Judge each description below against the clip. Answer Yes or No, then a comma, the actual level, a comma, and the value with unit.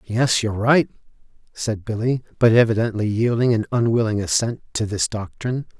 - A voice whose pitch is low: Yes, low, 115 Hz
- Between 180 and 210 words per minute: No, average, 145 wpm